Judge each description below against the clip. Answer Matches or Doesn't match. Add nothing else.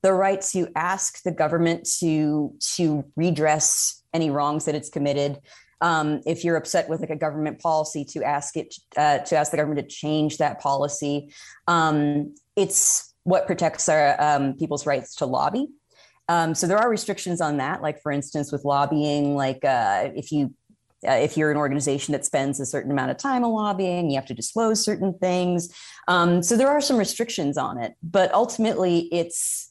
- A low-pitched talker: Doesn't match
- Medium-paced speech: Matches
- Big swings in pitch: Doesn't match